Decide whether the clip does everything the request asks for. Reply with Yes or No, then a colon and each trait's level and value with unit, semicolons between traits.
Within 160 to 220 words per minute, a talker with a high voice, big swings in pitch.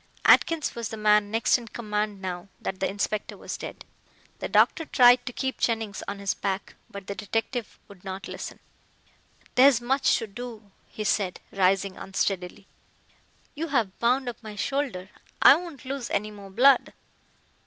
No: average, 165 wpm; high, 215 Hz; average, 3.9 semitones